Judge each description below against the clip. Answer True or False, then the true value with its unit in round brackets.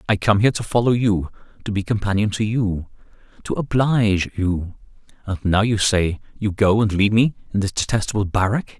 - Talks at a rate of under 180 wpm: True (170 wpm)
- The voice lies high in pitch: False (105 Hz)